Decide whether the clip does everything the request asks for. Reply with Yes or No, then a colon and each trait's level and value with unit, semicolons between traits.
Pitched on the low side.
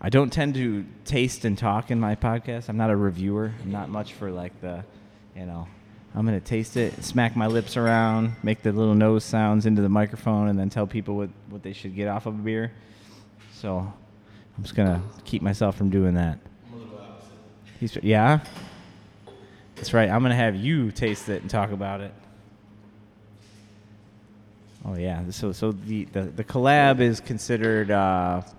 Yes: low, 105 Hz